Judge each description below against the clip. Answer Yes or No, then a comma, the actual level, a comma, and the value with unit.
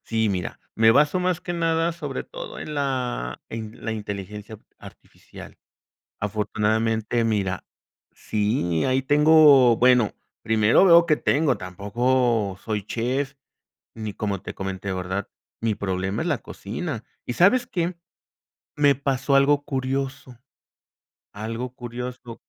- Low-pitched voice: Yes, low, 120 Hz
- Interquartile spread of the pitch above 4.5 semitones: Yes, average, 5.1 semitones